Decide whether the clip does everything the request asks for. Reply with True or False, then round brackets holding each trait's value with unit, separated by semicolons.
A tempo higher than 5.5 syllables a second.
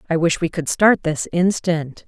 False (4.3 syllables/s)